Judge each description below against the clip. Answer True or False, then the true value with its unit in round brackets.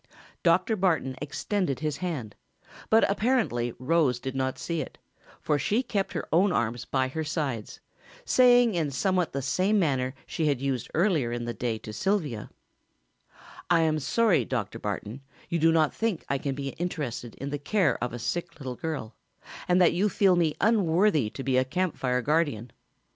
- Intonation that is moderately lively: False (6.0 semitones)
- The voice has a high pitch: False (155 Hz)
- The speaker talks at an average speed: True (180 wpm)